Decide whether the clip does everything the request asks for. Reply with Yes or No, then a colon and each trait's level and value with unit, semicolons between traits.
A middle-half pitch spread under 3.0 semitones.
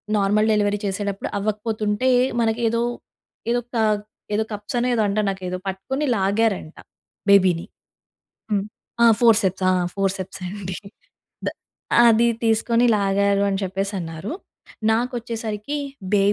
Yes: narrow, 2.4 semitones